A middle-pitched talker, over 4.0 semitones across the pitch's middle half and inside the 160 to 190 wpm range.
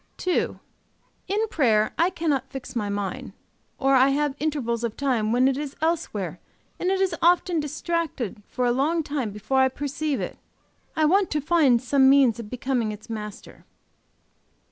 No: very high, 270 Hz; average, 5.0 semitones; average, 165 wpm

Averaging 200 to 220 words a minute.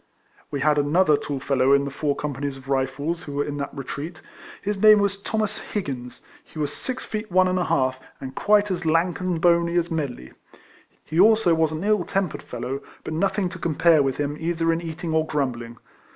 Yes: fast, 205 wpm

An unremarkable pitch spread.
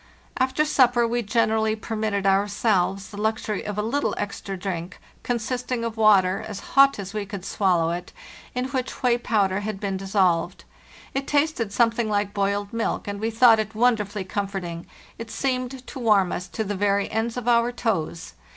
Yes: average, 3.2 semitones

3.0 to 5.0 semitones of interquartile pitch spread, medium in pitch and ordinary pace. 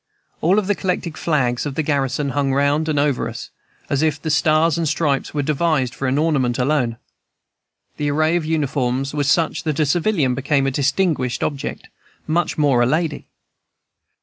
No: narrow, 2.6 semitones; medium, 145 Hz; average, 175 wpm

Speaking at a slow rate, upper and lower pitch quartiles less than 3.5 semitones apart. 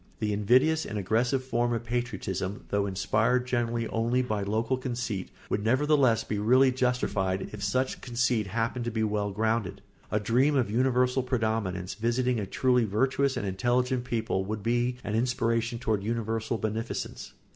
No: average, 155 wpm; average, 2.9 semitones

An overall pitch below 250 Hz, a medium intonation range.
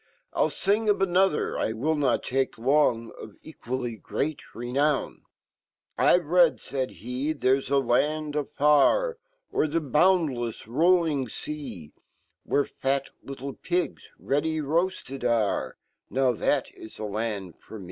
Yes: medium, 140 Hz; average, 4.3 semitones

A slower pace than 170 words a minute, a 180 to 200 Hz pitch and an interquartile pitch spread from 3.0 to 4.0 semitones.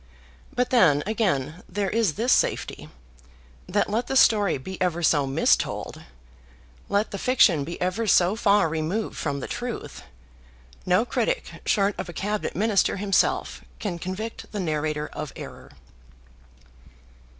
No: average, 140 wpm; high, 190 Hz; average, 4.9 semitones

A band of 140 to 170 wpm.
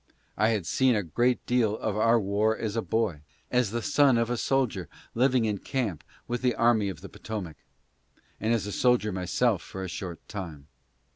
No: average, 195 wpm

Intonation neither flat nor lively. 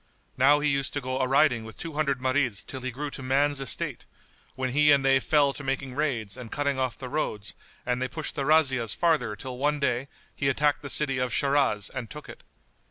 No: narrow, 2.3 semitones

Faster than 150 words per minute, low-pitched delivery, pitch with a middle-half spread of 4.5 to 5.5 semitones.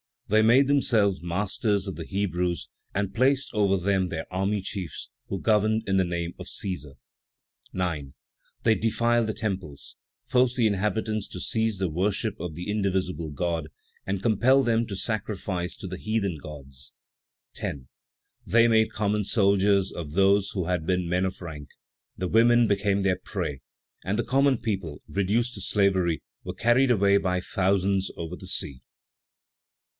No: average, 160 wpm; low, 100 Hz; average, 3.4 semitones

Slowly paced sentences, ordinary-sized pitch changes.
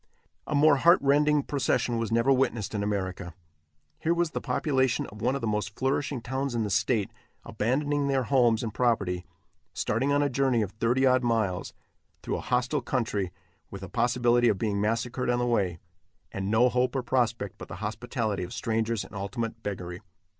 No: average, 185 wpm; average, 3.9 semitones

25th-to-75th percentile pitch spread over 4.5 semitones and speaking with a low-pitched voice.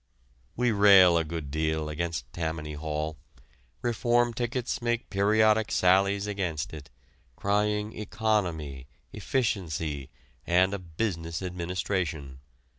Yes: average, 5.1 semitones; very low, 90 Hz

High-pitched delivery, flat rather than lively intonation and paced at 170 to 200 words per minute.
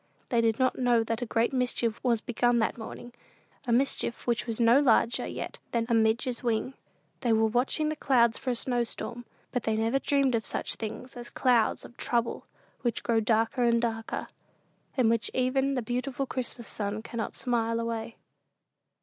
Yes: high, 235 Hz; narrow, 1.7 semitones; average, 185 wpm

